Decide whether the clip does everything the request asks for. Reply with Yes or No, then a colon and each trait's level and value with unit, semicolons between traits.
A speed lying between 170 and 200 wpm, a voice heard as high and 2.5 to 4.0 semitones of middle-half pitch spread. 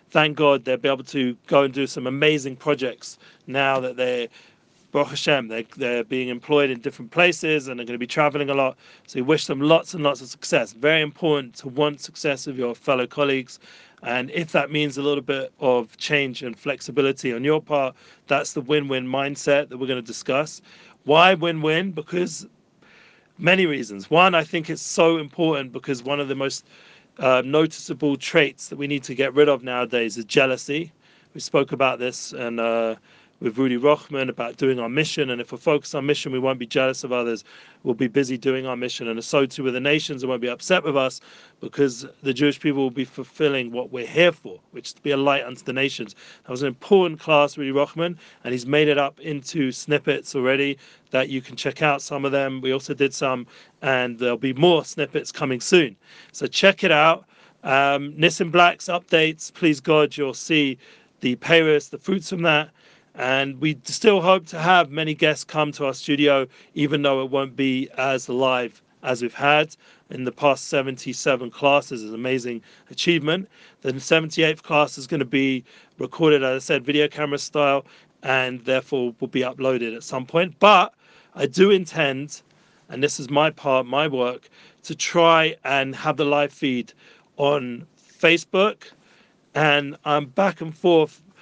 No: average, 195 wpm; medium, 140 Hz; average, 2.9 semitones